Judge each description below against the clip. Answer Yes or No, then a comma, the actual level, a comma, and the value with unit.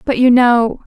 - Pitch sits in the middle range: No, high, 245 Hz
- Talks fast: No, average, 190 wpm